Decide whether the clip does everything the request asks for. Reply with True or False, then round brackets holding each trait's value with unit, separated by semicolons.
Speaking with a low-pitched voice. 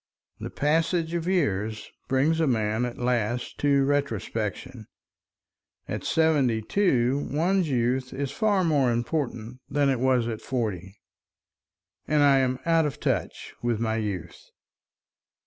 True (130 Hz)